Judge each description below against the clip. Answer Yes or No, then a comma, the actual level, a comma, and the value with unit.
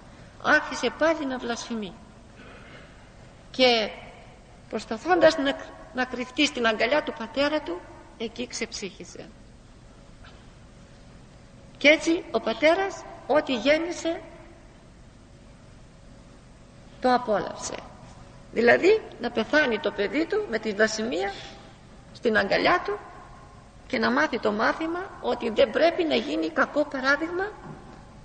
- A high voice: Yes, very high, 290 Hz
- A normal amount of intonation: No, wide, 5.7 semitones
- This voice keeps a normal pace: No, slow, 100 wpm